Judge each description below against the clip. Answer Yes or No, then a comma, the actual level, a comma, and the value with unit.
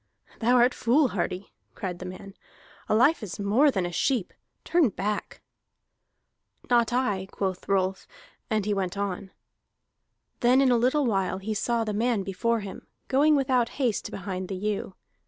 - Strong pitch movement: No, average, 4.3 semitones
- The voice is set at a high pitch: Yes, high, 210 Hz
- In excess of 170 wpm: No, average, 155 wpm